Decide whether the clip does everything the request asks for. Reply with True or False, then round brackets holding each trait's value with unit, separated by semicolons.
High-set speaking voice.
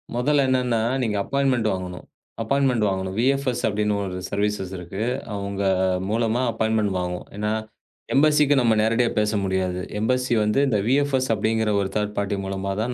False (110 Hz)